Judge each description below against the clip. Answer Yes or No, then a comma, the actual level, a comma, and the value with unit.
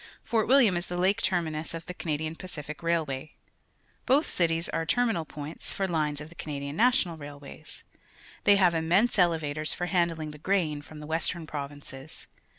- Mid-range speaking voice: Yes, medium, 165 Hz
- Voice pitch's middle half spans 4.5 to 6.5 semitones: No, average, 3.1 semitones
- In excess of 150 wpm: Yes, average, 165 wpm